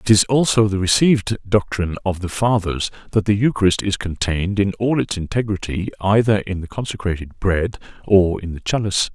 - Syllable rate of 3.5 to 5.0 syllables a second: No, 5.5 syllables/s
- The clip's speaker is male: Yes, male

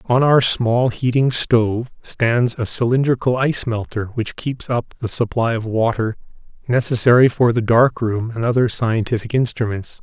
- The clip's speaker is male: Yes, male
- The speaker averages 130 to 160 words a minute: Yes, average, 155 wpm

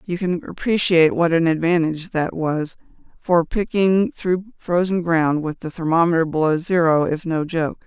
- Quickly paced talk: No, average, 160 wpm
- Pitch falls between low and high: Yes, medium, 170 Hz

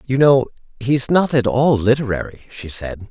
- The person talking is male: Yes, male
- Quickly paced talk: No, average, 175 wpm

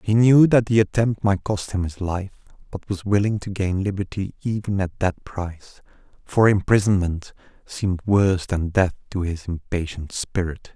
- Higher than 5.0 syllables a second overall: No, 4.8 syllables/s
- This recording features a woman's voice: No, male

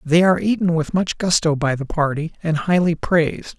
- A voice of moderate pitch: Yes, medium, 165 Hz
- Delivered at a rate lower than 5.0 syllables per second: No, 5.3 syllables/s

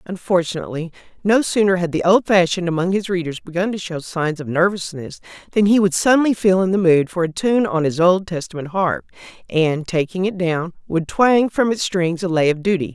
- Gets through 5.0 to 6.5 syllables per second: Yes, 5.5 syllables/s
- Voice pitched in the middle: Yes, medium, 180 Hz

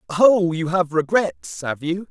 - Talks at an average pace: Yes, average, 170 wpm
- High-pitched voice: No, medium, 165 Hz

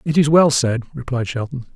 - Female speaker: No, male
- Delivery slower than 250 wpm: Yes, fast, 205 wpm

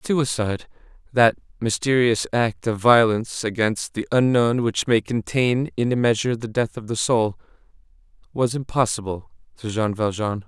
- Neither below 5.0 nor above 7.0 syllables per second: No, 4.7 syllables/s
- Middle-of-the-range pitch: No, low, 115 Hz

